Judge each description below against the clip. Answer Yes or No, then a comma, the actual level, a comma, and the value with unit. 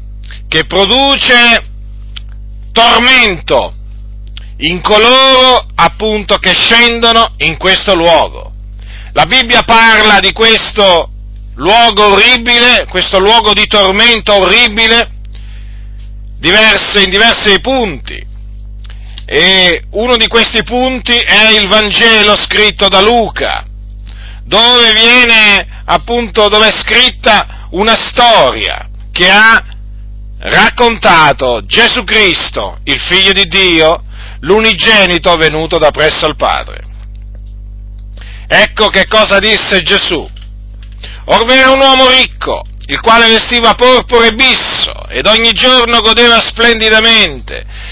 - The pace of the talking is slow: Yes, slow, 100 wpm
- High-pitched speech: Yes, high, 195 Hz